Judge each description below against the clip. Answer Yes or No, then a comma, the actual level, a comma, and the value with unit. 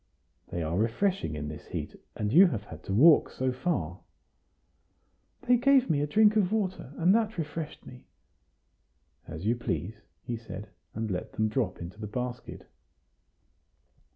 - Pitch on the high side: No, low, 125 Hz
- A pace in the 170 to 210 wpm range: No, average, 155 wpm